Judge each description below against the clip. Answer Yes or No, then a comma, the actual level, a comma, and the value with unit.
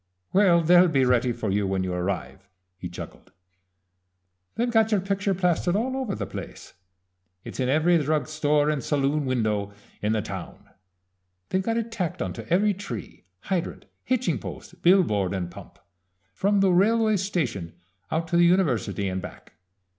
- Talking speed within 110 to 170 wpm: Yes, average, 160 wpm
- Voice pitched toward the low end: No, medium, 160 Hz